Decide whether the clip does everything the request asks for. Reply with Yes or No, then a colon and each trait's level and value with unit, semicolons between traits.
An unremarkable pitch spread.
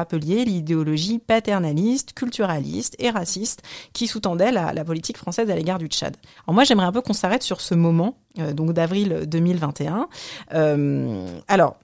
No: wide, 5.8 semitones